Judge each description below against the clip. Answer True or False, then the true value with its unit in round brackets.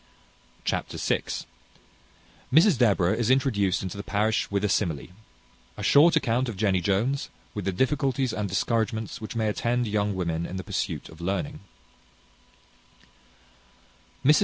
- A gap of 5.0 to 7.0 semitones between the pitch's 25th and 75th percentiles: False (4.3 semitones)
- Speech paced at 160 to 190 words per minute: False (135 wpm)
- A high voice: False (110 Hz)